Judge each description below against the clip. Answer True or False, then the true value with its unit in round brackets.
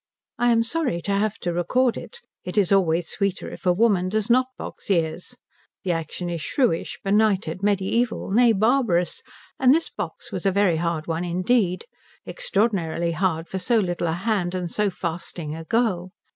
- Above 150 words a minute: True (175 wpm)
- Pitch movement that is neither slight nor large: True (4.3 semitones)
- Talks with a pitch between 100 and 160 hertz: False (190 Hz)